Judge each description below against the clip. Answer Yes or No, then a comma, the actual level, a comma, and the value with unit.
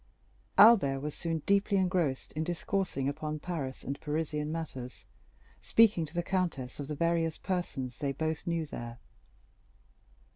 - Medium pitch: Yes, medium, 155 Hz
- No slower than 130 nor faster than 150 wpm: Yes, average, 140 wpm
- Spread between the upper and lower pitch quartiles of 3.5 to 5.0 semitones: Yes, average, 3.8 semitones